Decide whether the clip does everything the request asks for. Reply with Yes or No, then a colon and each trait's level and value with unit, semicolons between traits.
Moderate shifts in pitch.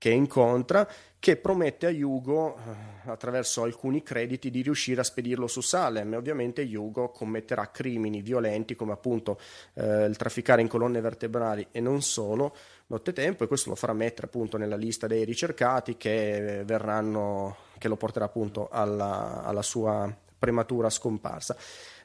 Yes: average, 3.0 semitones